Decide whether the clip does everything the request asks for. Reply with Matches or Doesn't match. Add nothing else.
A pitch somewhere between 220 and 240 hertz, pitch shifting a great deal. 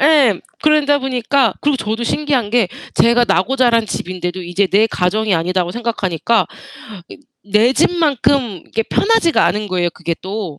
Matches